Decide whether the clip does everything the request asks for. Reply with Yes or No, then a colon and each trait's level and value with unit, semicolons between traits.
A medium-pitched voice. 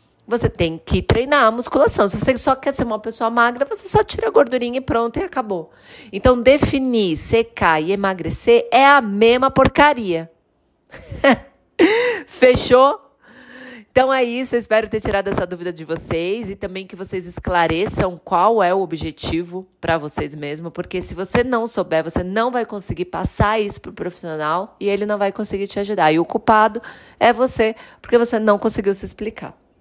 No: high, 215 Hz